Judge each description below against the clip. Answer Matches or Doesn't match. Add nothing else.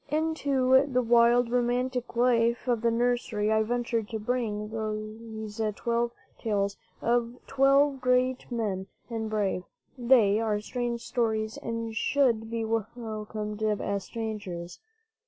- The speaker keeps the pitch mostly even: Matches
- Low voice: Doesn't match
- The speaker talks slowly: Matches